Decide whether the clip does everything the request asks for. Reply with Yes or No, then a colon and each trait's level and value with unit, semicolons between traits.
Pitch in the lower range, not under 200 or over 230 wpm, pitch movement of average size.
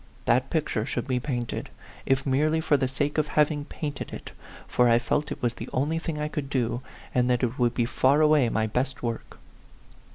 Yes: low, 130 Hz; fast, 205 wpm; average, 3.5 semitones